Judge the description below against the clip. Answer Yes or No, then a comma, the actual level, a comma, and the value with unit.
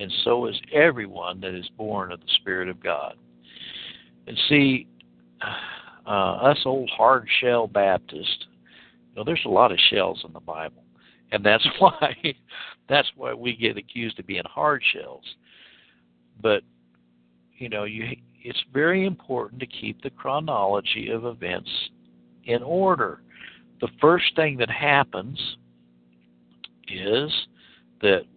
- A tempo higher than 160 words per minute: No, slow, 135 wpm